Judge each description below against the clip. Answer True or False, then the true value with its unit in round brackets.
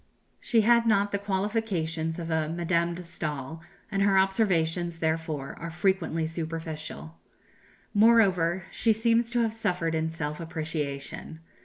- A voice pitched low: False (170 Hz)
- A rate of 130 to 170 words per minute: True (135 wpm)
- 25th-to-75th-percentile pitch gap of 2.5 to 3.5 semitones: False (3.9 semitones)